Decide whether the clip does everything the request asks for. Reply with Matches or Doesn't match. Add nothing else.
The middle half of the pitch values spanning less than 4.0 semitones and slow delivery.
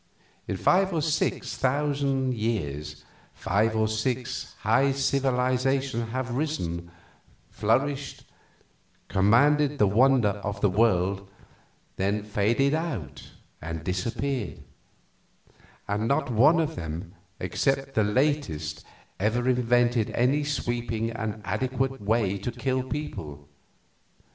Doesn't match